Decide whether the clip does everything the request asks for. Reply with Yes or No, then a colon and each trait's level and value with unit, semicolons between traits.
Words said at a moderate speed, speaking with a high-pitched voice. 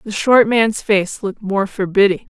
Yes: average, 180 wpm; high, 205 Hz